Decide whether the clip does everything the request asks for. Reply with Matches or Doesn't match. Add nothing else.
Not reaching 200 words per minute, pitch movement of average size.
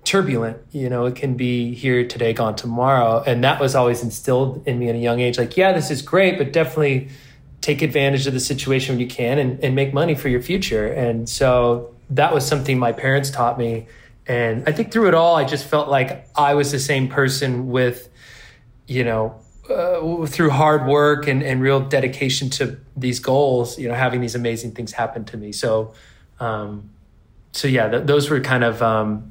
Doesn't match